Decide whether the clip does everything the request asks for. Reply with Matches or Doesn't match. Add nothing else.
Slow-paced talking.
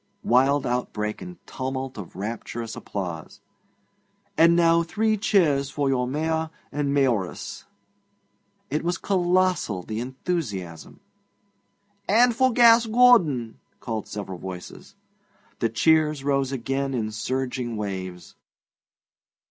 Matches